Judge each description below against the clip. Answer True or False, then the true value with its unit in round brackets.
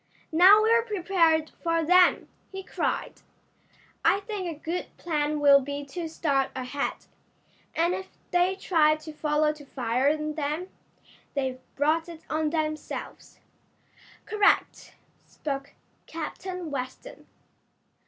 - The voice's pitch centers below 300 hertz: False (315 Hz)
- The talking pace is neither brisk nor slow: False (120 wpm)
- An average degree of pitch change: True (3.7 semitones)